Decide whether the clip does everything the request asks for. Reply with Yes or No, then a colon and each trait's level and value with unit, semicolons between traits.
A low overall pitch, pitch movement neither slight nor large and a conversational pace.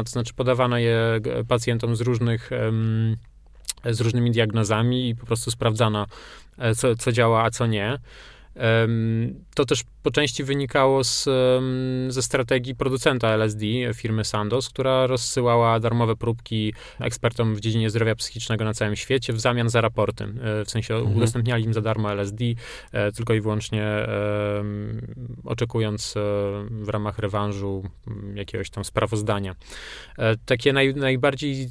No: low, 115 Hz; narrow, 2.3 semitones; average, 130 wpm